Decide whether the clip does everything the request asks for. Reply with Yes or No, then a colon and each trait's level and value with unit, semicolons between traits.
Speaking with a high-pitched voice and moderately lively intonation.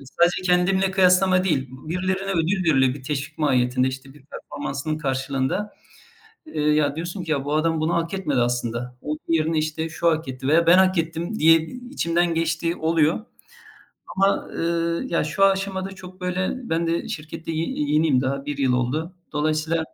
No: medium, 160 Hz; average, 3.8 semitones